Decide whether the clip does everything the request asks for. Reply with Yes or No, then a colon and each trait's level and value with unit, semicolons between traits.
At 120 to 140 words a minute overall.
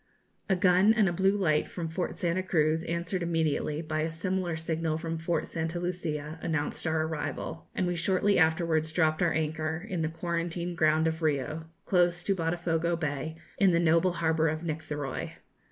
No: average, 175 wpm